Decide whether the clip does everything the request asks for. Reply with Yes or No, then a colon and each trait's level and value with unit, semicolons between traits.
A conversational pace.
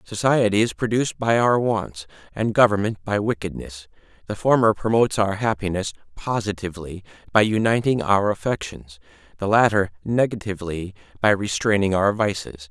No: slow, 125 wpm